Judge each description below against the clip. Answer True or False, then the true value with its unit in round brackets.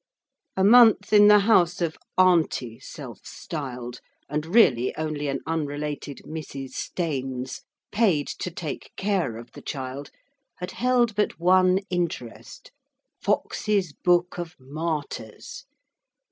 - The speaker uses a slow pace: True (120 wpm)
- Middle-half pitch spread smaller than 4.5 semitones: False (5.1 semitones)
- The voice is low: False (165 Hz)